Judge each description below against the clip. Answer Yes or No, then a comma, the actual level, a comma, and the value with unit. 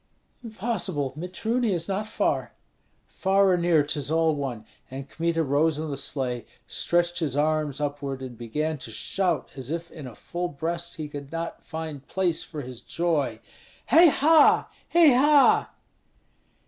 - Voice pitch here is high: No, medium, 160 Hz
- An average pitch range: Yes, average, 4.0 semitones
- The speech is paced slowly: No, average, 155 wpm